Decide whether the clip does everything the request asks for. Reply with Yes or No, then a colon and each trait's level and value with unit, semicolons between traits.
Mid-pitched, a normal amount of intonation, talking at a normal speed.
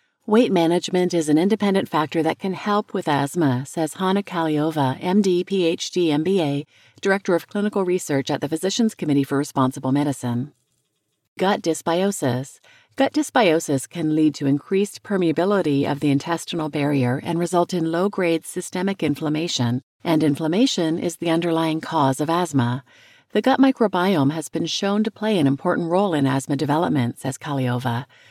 Yes: medium, 165 Hz; average, 4.8 semitones; average, 150 wpm